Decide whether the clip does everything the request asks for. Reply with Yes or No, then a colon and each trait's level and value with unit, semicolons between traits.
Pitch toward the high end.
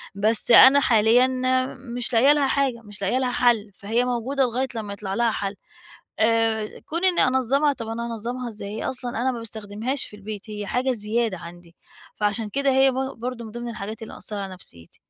Yes: high, 230 Hz